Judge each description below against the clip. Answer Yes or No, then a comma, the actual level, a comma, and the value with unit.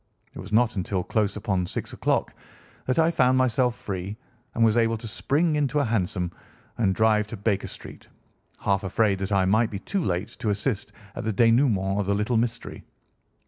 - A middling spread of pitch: Yes, average, 3.5 semitones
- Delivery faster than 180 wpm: Yes, average, 190 wpm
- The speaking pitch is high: No, low, 110 Hz